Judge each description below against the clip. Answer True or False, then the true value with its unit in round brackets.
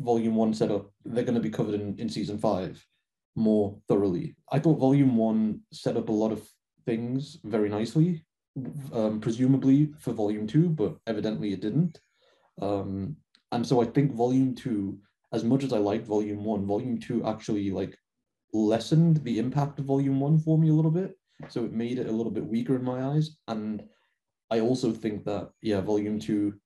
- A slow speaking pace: False (185 wpm)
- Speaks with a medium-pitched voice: False (115 Hz)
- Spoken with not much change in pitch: False (4.4 semitones)